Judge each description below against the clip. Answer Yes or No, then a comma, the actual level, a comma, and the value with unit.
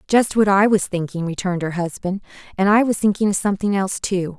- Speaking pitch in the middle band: No, high, 195 Hz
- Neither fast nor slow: No, fast, 220 wpm